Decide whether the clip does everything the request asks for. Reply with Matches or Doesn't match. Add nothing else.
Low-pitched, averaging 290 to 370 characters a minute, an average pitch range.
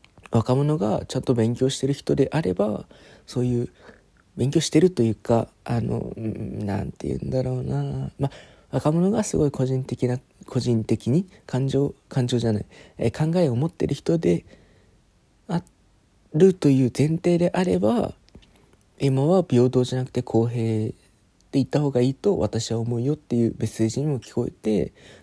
Matches